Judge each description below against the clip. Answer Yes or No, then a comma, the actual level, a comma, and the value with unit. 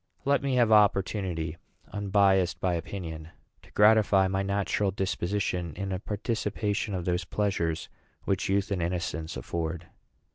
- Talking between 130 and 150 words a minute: Yes, slow, 135 wpm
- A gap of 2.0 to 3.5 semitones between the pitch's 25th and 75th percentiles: Yes, average, 2.8 semitones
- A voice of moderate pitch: No, very low, 95 Hz